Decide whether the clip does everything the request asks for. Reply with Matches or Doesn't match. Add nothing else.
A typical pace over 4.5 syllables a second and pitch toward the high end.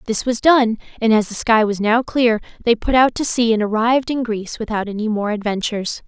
Matches